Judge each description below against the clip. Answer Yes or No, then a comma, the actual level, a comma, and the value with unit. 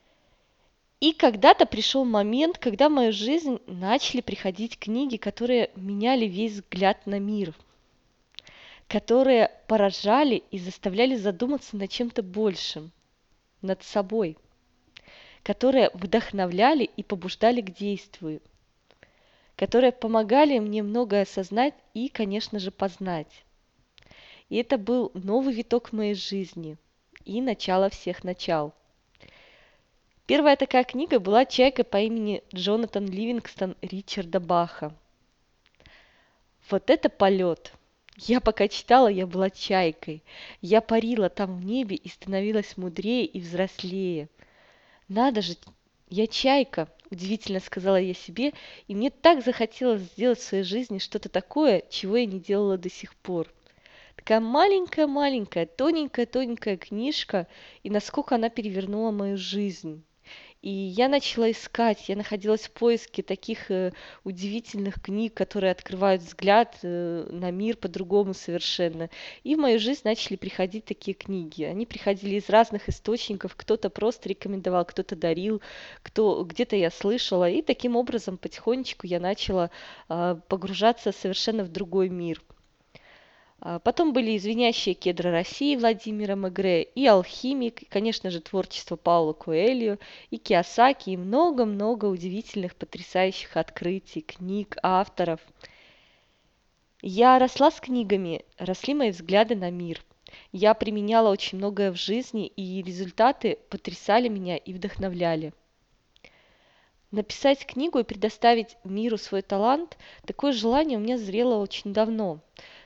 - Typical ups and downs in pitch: Yes, average, 3.9 semitones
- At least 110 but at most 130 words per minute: Yes, average, 120 wpm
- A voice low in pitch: No, high, 205 Hz